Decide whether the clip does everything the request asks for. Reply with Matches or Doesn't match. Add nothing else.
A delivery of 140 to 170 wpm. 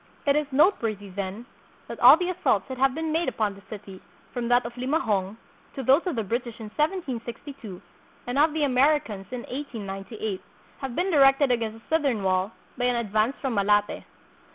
Doesn't match